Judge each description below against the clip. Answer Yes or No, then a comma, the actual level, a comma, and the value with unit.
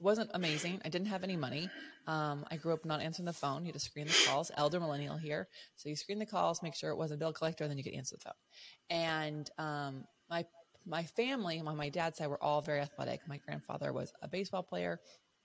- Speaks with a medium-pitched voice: Yes, medium, 155 Hz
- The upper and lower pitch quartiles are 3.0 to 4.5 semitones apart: No, narrow, 2.5 semitones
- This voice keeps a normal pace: No, fast, 235 wpm